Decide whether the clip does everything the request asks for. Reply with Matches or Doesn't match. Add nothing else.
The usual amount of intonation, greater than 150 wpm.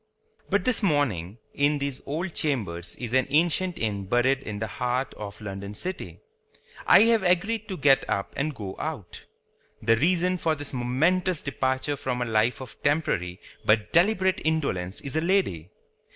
Doesn't match